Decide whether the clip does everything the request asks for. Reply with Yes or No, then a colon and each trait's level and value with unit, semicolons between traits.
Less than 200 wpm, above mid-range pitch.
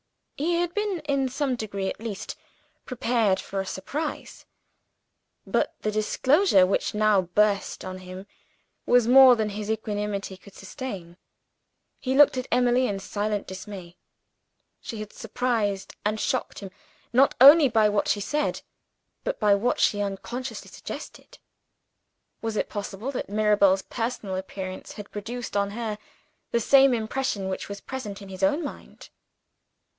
Yes: average, 145 wpm; high, 215 Hz